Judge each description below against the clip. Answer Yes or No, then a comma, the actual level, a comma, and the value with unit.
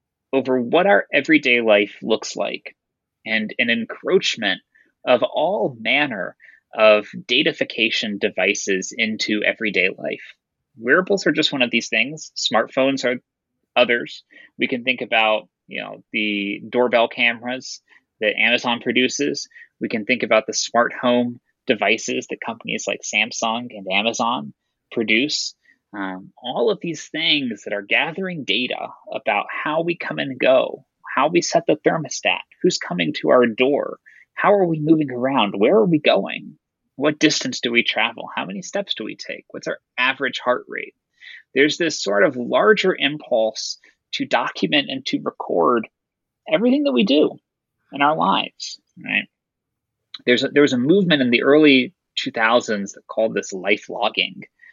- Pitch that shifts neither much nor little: No, wide, 5.7 semitones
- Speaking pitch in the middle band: No, low, 125 Hz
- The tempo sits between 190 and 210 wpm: No, average, 155 wpm